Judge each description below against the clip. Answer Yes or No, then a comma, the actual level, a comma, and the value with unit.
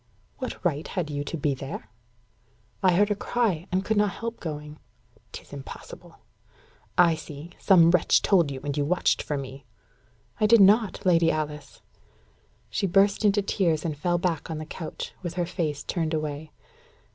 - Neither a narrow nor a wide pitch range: Yes, average, 4.2 semitones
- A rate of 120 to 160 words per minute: No, average, 170 wpm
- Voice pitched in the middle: Yes, medium, 165 Hz